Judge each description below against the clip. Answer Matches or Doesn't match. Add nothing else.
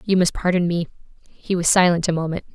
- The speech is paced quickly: Matches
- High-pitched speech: Doesn't match